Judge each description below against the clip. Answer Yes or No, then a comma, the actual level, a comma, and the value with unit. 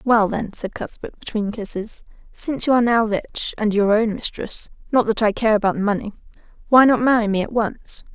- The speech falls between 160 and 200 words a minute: Yes, average, 190 wpm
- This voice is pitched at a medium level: No, high, 220 Hz